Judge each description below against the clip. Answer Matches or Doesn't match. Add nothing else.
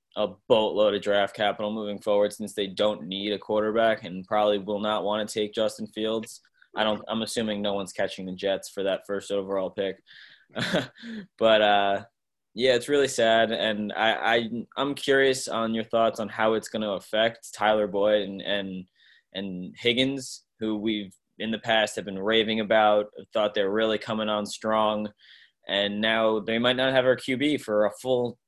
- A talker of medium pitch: Doesn't match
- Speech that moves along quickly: Doesn't match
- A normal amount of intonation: Doesn't match